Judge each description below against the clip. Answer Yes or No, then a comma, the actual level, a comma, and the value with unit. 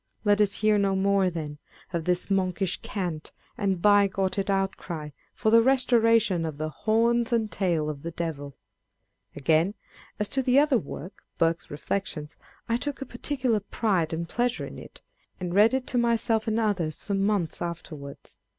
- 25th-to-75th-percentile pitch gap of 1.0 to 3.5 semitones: No, average, 5.1 semitones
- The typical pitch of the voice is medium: No, high, 195 Hz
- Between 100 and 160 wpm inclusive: No, average, 170 wpm